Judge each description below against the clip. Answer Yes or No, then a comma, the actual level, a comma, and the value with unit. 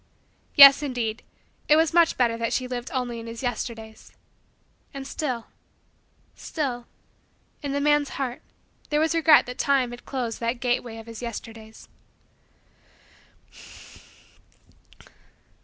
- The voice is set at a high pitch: Yes, very high, 250 Hz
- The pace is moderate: No, slow, 125 wpm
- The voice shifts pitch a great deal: No, average, 3.4 semitones